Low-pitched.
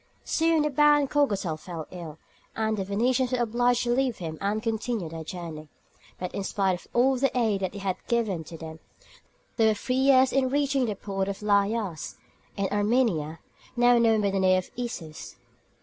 No: high, 215 Hz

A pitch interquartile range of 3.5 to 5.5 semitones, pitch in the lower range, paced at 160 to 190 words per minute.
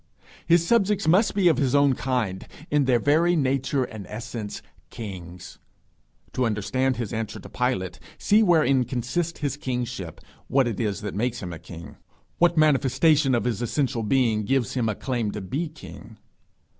Yes: average, 5.1 semitones; low, 130 Hz; average, 170 wpm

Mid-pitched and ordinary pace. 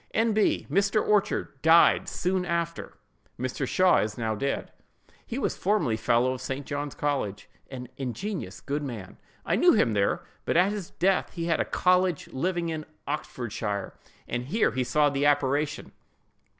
Yes: medium, 145 Hz; average, 155 wpm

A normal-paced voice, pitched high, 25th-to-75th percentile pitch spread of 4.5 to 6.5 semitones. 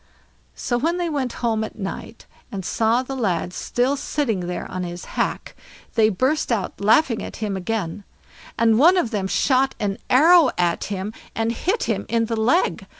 Yes: average, 180 wpm; high, 225 Hz; average, 4.8 semitones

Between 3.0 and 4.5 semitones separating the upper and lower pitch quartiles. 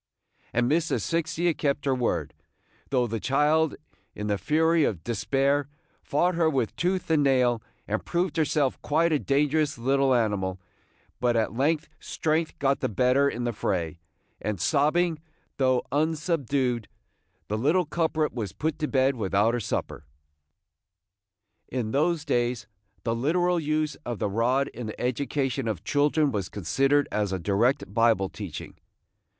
No: average, 5.0 semitones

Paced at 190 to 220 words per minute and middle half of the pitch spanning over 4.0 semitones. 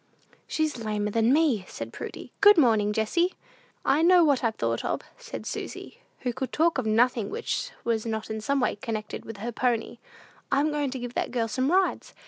Yes: average, 195 wpm; average, 5.3 semitones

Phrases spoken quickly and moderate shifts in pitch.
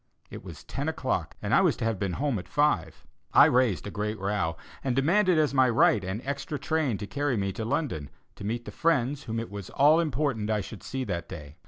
No: fast, 230 wpm; wide, 5.9 semitones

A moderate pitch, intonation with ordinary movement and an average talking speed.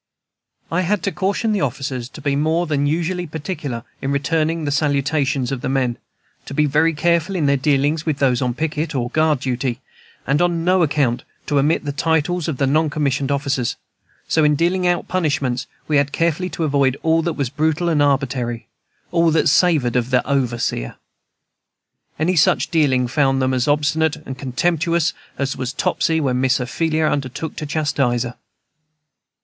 Yes: medium, 145 Hz; average, 3.3 semitones; average, 175 wpm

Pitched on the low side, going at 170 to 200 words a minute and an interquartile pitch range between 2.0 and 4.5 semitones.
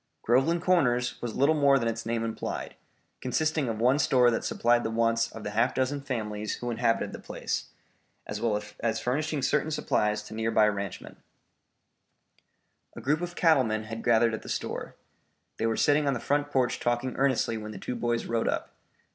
Yes: low, 120 Hz; average, 190 wpm; average, 3.5 semitones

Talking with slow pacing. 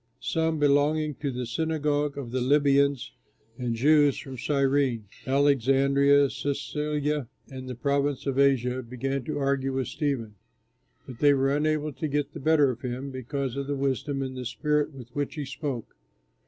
No: average, 160 wpm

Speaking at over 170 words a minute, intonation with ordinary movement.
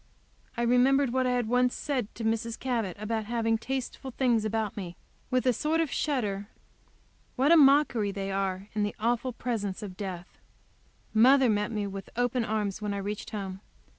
Yes: average, 180 wpm; average, 3.5 semitones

